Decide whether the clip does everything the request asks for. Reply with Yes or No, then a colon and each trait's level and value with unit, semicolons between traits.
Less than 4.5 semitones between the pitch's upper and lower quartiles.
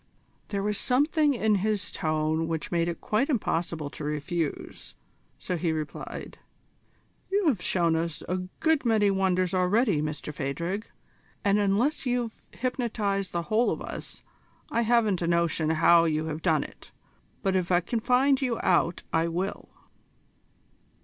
No: wide, 5.5 semitones